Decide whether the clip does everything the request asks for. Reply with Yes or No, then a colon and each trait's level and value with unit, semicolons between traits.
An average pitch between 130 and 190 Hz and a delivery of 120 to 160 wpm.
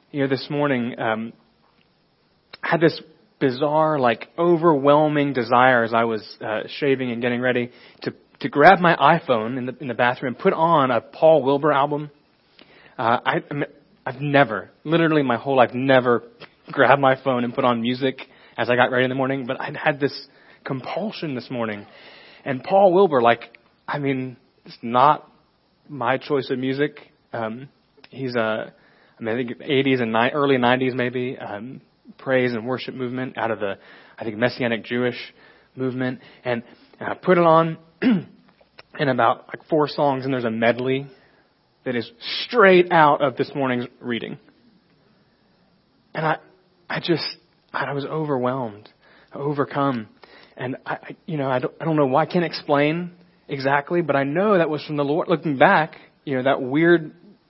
No: low, 135 Hz; average, 170 wpm